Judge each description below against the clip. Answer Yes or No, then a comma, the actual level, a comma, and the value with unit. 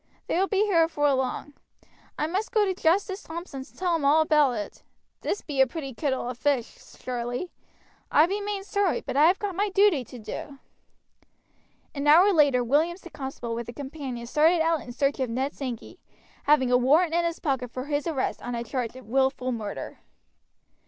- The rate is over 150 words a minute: Yes, average, 200 wpm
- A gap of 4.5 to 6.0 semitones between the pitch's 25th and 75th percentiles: Yes, average, 5.1 semitones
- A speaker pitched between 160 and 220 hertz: No, very high, 290 Hz